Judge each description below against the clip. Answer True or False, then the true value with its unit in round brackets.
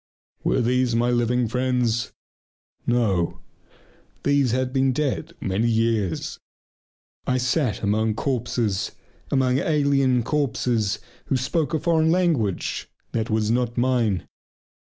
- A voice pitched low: True (125 Hz)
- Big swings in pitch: False (3.0 semitones)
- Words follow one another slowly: True (110 wpm)